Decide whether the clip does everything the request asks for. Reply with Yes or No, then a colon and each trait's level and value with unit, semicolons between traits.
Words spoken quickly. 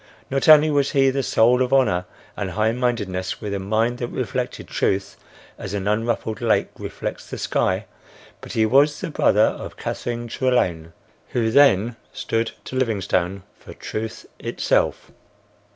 No: average, 150 wpm